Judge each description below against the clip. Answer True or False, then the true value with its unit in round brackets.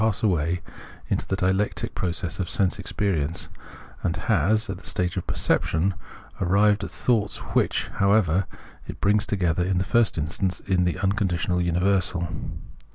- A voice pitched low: True (95 Hz)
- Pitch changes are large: False (2.5 semitones)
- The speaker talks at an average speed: True (150 wpm)